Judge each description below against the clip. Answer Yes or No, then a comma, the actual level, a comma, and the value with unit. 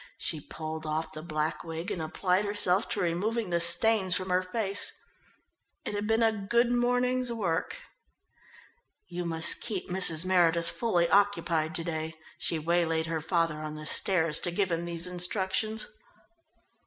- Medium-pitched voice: Yes, medium, 175 Hz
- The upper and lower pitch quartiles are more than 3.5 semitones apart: Yes, average, 3.9 semitones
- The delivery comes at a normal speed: Yes, average, 155 wpm